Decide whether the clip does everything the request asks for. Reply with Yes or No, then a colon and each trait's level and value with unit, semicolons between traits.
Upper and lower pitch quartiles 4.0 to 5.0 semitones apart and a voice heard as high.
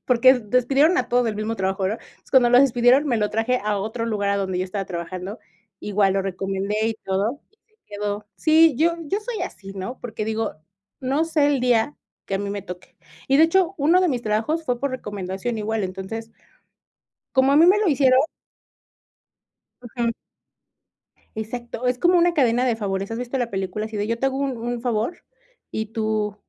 Yes: average, 4.5 semitones; high, 230 Hz